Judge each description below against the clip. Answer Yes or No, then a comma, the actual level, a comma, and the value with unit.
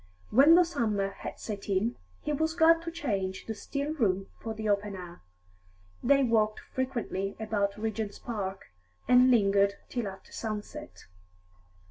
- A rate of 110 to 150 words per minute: Yes, average, 145 wpm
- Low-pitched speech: No, high, 215 Hz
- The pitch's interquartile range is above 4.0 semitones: Yes, average, 4.7 semitones